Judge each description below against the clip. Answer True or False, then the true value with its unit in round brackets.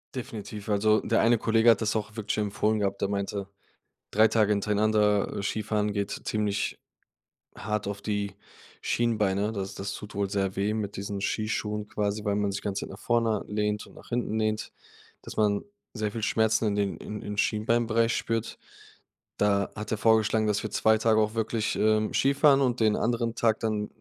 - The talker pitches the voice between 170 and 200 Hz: False (105 Hz)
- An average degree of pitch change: False (1.4 semitones)